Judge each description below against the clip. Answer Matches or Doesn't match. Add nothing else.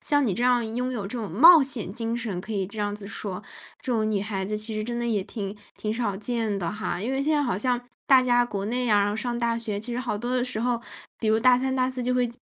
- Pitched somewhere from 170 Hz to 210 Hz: Doesn't match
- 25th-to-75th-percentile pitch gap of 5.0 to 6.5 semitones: Doesn't match